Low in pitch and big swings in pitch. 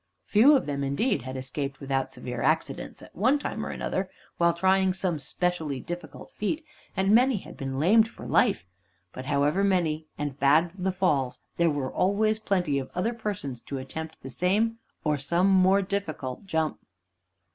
No: medium, 170 Hz; wide, 5.9 semitones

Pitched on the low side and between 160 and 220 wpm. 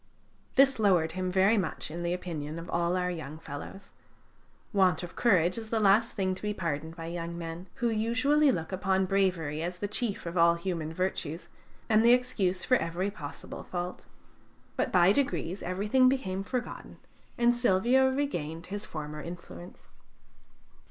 No: medium, 185 Hz; average, 165 wpm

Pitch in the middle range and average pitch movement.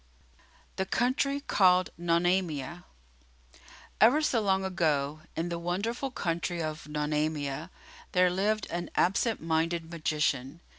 Yes: medium, 175 Hz; average, 3.4 semitones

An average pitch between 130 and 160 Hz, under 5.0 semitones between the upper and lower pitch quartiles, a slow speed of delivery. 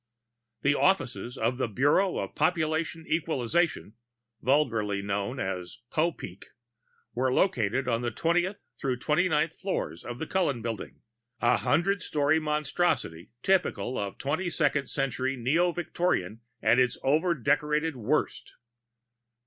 No: medium, 140 Hz; wide, 5.6 semitones; slow, 125 wpm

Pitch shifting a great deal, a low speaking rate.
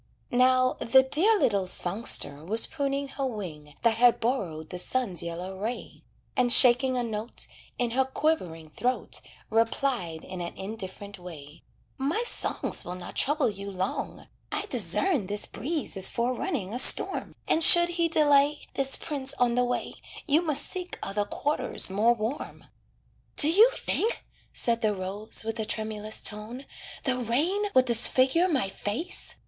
No: wide, 5.7 semitones; average, 155 wpm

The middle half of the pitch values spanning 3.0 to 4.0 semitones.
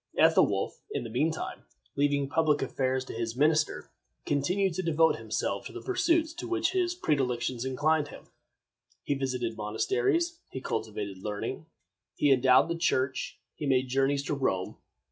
No: average, 4.4 semitones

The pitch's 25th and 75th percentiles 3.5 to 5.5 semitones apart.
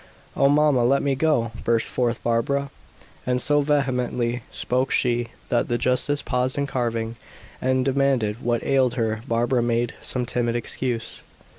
No: narrow, 2.5 semitones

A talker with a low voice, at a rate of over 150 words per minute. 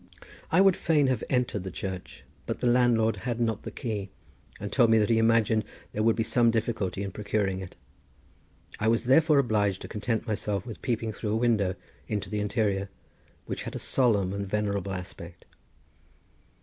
Yes: low, 110 Hz; average, 180 wpm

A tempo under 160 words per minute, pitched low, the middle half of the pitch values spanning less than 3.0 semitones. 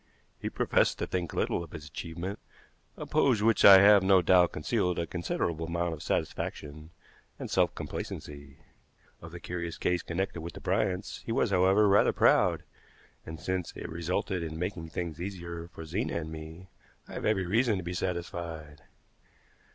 No: average, 170 wpm; very low, 85 Hz; narrow, 2.6 semitones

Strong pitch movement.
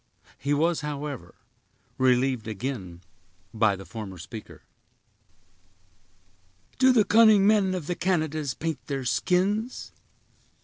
Yes: wide, 8.2 semitones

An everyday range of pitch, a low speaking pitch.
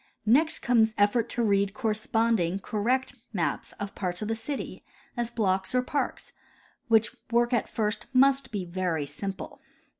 No: average, 3.5 semitones; high, 220 Hz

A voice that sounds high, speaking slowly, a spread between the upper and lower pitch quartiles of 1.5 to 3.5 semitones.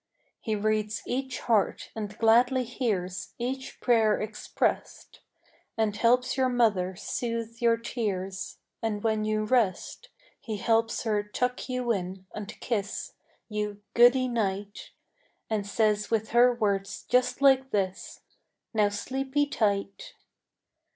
Yes: high, 220 Hz; slow, 125 wpm; average, 3.0 semitones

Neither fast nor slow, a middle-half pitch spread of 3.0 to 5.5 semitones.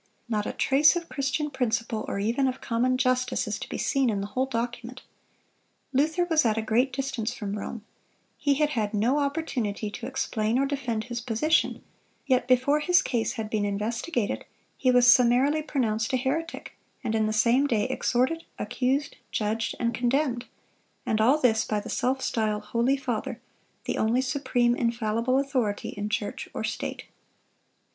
Yes: average, 170 wpm; average, 3.5 semitones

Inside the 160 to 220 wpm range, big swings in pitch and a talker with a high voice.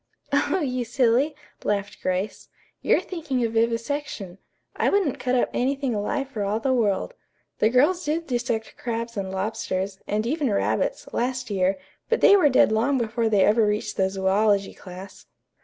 No: average, 165 wpm; average, 4.7 semitones; high, 230 Hz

